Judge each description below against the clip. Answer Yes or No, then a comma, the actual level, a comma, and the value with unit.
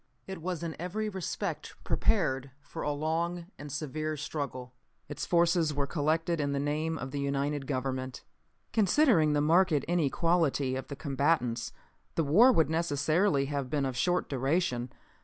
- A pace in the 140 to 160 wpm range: Yes, average, 155 wpm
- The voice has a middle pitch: Yes, medium, 150 Hz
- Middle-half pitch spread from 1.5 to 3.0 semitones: No, average, 3.5 semitones